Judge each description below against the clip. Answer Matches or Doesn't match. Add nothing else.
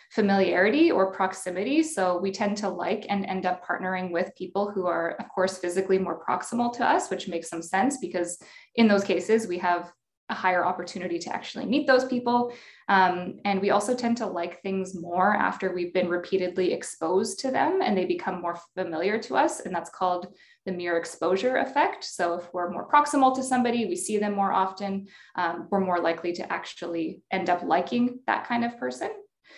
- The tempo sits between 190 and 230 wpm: Matches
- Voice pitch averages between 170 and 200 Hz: Matches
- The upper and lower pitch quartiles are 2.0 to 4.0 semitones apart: Matches